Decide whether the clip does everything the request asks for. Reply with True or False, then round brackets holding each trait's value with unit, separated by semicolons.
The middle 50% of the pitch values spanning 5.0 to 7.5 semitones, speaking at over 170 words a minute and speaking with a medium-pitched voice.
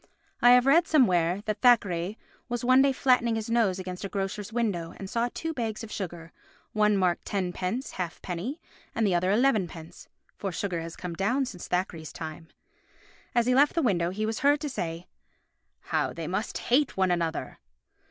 False (5.4 semitones; 180 wpm; 205 Hz)